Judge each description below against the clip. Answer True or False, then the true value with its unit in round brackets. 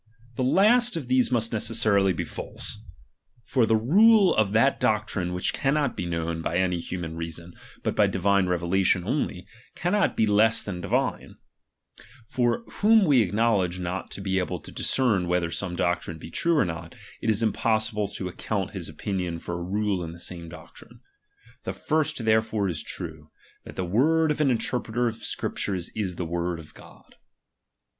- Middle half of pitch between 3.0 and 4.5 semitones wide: False (5.1 semitones)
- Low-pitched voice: True (100 Hz)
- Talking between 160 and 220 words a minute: True (175 wpm)